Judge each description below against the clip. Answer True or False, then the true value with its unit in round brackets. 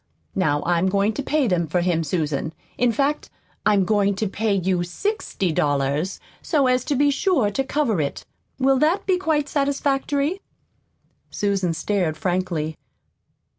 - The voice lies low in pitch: False (205 Hz)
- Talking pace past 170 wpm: False (150 wpm)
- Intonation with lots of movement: True (8.1 semitones)